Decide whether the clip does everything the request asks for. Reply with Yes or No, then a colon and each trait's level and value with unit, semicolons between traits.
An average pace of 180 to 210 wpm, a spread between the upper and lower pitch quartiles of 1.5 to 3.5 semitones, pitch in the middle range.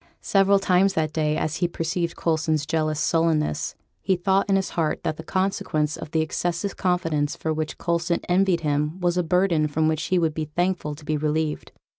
Yes: average, 195 wpm; narrow, 2.6 semitones; medium, 165 Hz